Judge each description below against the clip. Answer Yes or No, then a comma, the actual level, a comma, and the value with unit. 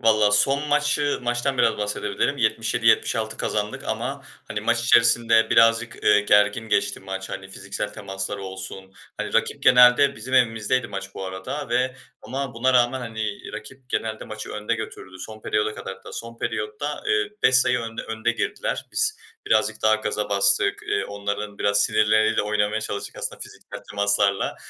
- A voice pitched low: Yes, low, 110 Hz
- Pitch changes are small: No, average, 3.0 semitones